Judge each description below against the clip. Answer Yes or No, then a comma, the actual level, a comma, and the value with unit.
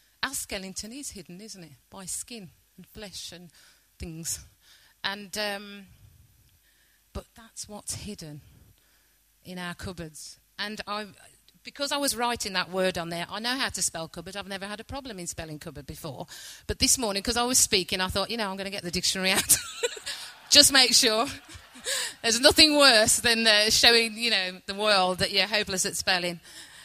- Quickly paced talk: No, average, 185 wpm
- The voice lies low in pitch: No, high, 200 Hz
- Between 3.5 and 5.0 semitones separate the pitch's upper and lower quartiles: Yes, average, 4.4 semitones